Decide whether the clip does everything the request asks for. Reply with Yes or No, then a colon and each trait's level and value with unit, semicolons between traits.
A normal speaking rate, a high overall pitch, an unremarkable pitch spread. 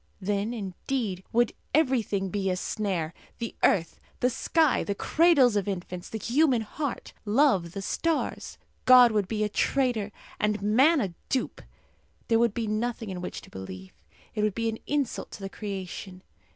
Yes: average, 165 wpm; high, 215 Hz; average, 4.2 semitones